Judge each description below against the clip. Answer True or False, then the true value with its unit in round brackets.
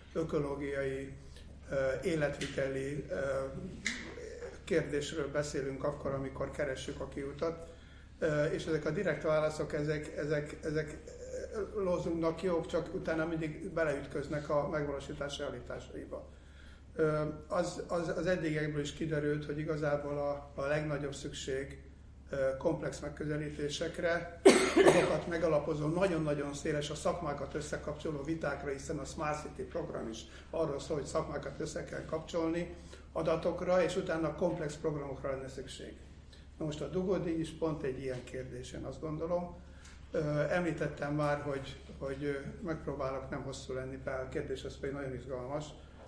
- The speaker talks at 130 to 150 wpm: False (120 wpm)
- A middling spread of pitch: True (3.0 semitones)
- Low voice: False (150 Hz)